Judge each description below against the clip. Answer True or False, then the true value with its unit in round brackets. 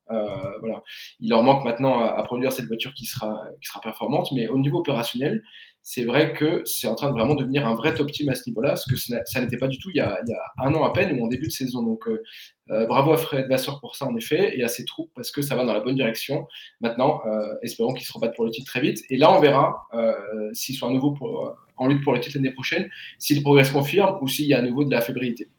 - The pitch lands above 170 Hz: False (130 Hz)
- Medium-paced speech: False (280 wpm)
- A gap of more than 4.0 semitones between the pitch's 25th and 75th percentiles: False (3.5 semitones)